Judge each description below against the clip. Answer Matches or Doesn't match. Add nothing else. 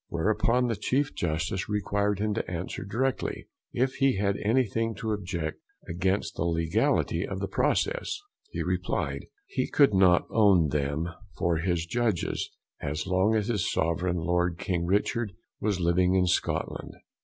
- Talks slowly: Doesn't match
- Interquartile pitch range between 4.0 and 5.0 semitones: Matches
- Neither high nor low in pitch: Doesn't match